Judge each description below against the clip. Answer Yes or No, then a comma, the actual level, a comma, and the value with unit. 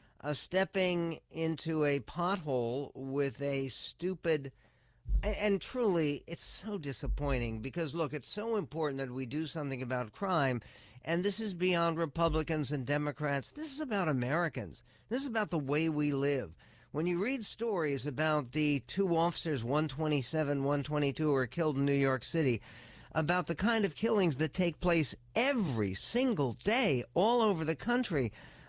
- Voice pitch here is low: No, medium, 155 Hz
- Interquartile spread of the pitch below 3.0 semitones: No, average, 4.4 semitones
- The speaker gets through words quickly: No, average, 155 wpm